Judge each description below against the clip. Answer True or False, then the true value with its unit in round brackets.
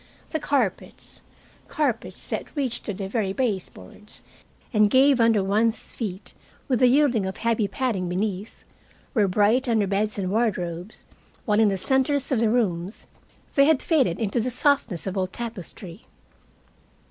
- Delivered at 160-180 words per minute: False (150 wpm)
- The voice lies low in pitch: False (220 Hz)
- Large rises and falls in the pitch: False (4.6 semitones)